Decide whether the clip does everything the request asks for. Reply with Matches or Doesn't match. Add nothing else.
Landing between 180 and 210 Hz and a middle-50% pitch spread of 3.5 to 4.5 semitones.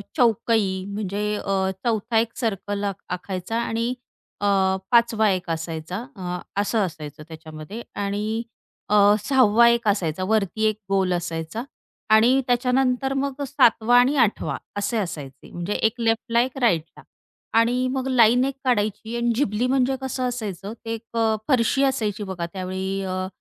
Doesn't match